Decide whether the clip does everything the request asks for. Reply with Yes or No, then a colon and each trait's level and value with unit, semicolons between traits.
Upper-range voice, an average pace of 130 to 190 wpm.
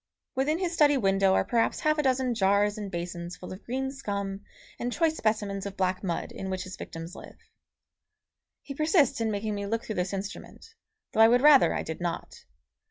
No: high, 210 Hz; average, 200 wpm